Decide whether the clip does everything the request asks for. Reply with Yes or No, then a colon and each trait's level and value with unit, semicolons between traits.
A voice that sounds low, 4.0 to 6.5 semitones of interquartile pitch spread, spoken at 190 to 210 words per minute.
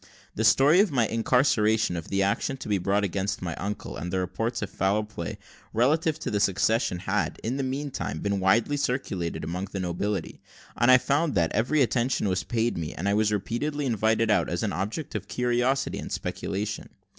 Yes: low, 110 Hz; average, 4.5 semitones; average, 195 wpm